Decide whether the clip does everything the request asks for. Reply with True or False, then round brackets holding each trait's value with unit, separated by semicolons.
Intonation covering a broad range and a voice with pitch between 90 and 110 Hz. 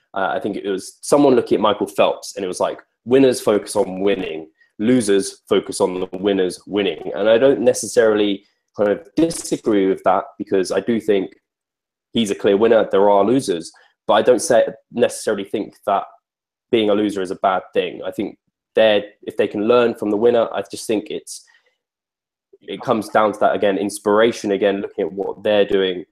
True (8.5 semitones; 105 Hz)